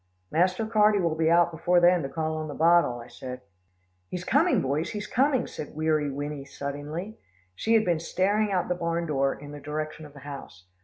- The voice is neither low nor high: Yes, medium, 160 Hz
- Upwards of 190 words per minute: Yes, fast, 205 wpm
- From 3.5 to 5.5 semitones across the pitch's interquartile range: Yes, average, 3.9 semitones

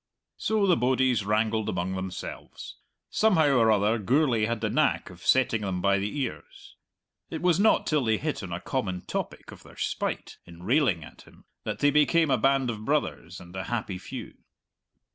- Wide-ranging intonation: Yes, wide, 6.7 semitones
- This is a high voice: No, low, 115 Hz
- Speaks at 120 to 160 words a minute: No, average, 185 wpm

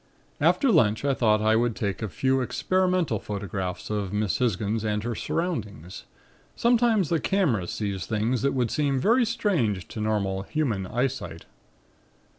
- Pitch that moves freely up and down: Yes, wide, 6.5 semitones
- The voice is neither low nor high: No, low, 110 Hz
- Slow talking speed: No, average, 150 wpm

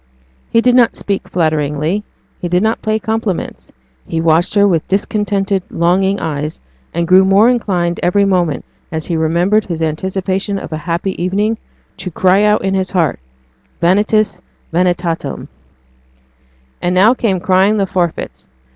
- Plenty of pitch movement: No, average, 3.1 semitones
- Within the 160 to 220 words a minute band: No, average, 145 wpm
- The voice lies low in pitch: No, medium, 185 Hz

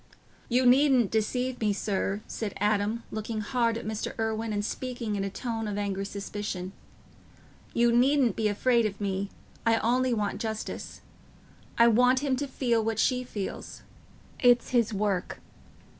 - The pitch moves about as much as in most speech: Yes, average, 3.0 semitones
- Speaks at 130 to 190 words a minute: Yes, average, 155 wpm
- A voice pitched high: Yes, high, 225 Hz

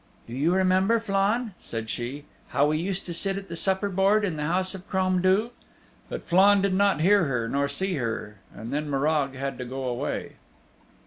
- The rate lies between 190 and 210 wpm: Yes, average, 200 wpm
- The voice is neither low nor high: Yes, medium, 180 Hz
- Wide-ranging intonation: Yes, wide, 5.9 semitones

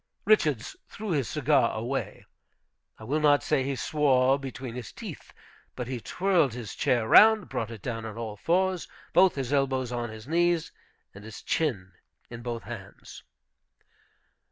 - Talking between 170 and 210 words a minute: No, average, 155 wpm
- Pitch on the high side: No, low, 130 Hz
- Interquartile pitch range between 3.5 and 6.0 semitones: Yes, average, 4.8 semitones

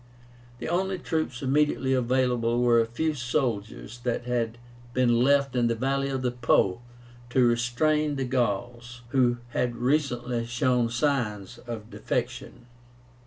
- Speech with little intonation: Yes, narrow, 2.3 semitones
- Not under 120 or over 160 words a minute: Yes, slow, 135 wpm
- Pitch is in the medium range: No, low, 125 Hz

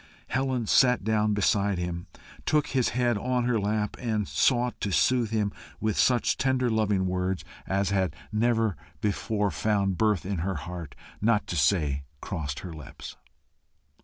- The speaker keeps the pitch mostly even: No, average, 4.0 semitones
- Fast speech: No, average, 155 wpm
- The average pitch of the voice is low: Yes, low, 105 Hz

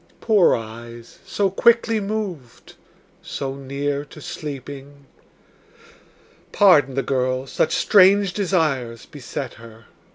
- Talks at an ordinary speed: No, slow, 100 wpm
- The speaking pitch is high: No, medium, 140 Hz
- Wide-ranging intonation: Yes, wide, 7.0 semitones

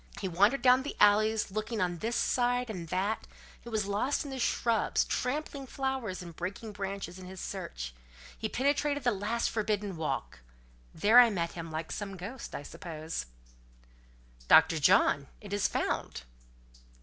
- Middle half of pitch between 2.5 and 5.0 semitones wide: No, wide, 5.5 semitones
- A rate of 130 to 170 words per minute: Yes, average, 160 wpm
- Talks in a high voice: Yes, high, 205 Hz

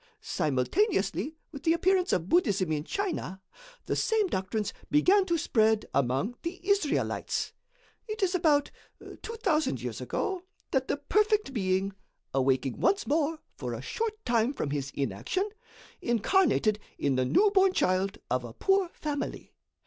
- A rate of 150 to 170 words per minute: No, average, 140 wpm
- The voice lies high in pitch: Yes, very high, 285 Hz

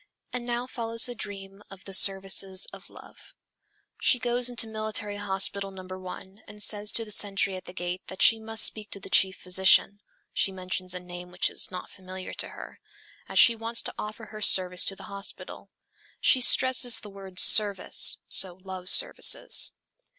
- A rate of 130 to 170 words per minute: No, average, 180 wpm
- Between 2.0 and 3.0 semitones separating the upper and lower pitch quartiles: Yes, average, 2.7 semitones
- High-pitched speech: Yes, high, 200 Hz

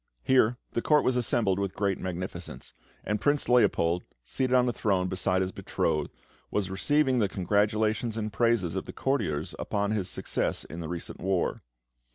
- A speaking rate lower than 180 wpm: Yes, average, 170 wpm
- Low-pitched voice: Yes, low, 105 Hz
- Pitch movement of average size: Yes, average, 4.6 semitones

